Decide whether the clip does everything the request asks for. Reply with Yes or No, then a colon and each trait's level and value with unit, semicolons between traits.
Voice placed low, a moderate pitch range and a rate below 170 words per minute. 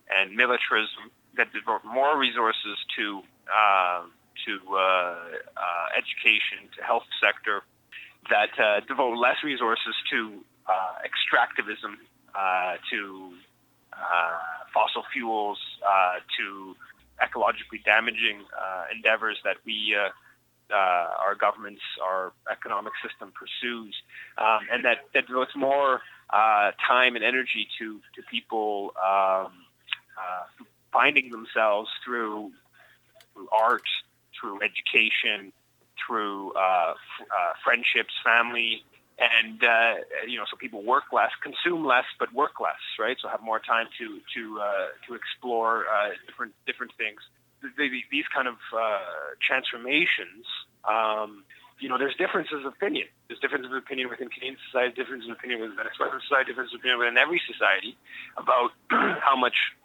Yes: low, 110 Hz; average, 4.1 semitones; slow, 135 wpm